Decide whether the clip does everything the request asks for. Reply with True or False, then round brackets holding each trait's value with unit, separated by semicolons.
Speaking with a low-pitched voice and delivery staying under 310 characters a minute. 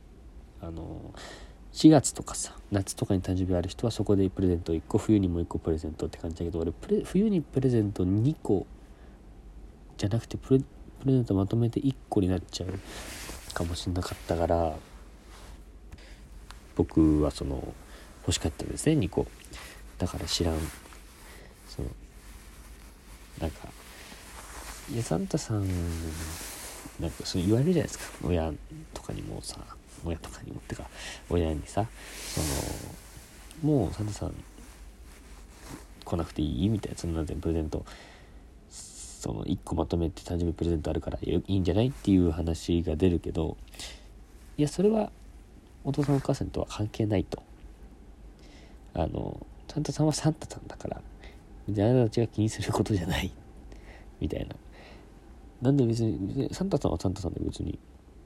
True (85 Hz; 300 characters per minute)